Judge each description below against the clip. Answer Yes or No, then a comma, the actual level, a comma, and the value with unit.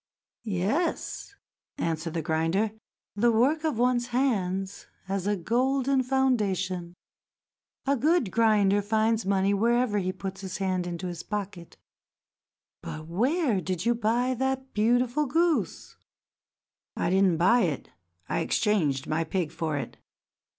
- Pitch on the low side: No, high, 205 Hz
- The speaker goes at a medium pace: No, slow, 130 wpm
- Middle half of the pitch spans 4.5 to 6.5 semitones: Yes, wide, 5.4 semitones